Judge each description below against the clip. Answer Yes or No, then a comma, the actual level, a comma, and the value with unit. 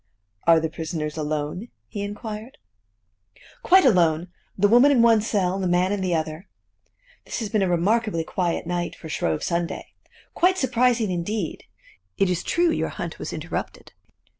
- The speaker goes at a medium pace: Yes, average, 165 wpm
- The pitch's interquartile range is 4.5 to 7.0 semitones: Yes, average, 4.9 semitones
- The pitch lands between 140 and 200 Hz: Yes, medium, 185 Hz